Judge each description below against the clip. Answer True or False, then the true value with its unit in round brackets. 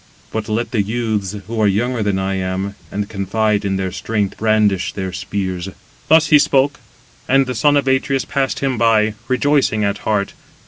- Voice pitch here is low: True (110 Hz)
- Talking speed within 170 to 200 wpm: True (180 wpm)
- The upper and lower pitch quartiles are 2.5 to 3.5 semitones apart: False (4.4 semitones)